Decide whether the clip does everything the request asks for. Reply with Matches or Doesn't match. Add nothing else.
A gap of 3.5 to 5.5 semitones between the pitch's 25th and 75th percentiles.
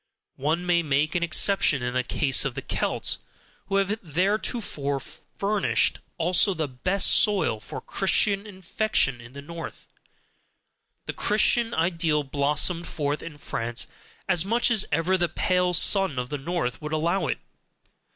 Matches